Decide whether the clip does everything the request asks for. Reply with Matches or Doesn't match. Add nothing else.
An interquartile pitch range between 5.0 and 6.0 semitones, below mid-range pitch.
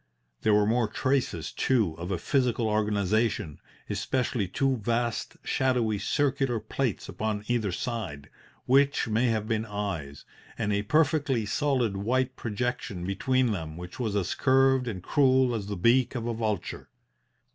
Doesn't match